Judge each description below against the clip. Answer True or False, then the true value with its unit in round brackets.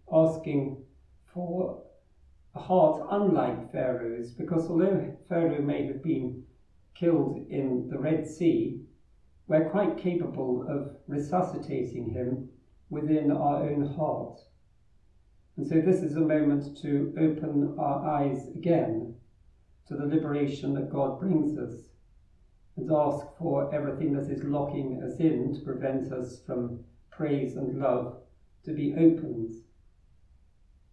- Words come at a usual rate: False (125 wpm)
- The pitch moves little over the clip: False (3.9 semitones)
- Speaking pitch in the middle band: True (145 Hz)